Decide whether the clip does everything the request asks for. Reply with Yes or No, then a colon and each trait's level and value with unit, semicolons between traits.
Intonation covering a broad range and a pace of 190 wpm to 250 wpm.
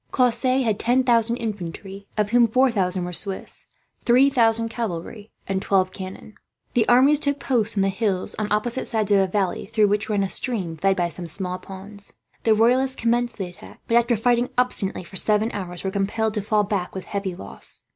No: average, 3.6 semitones; average, 200 wpm